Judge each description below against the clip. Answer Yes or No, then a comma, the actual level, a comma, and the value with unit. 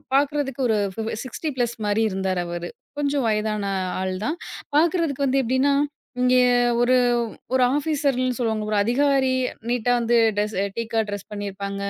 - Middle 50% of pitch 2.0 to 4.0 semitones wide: No, average, 4.8 semitones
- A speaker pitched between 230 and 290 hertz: Yes, high, 240 Hz